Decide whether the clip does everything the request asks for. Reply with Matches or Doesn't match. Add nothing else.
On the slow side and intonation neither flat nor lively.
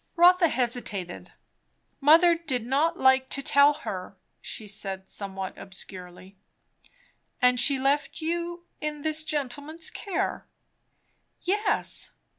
Doesn't match